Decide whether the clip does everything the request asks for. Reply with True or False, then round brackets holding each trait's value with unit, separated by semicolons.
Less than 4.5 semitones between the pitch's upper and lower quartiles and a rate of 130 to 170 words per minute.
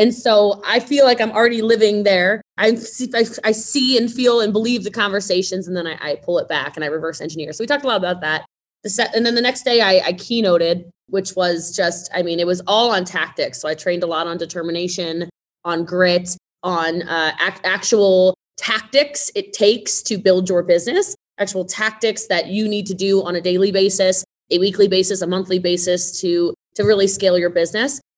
False (3.8 semitones; 200 wpm)